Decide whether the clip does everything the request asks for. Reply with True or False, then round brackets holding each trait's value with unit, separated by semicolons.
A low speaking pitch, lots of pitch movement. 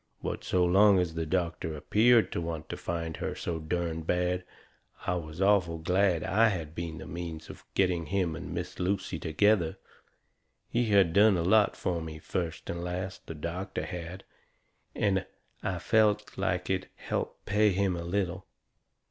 False (90 Hz; 2.8 semitones)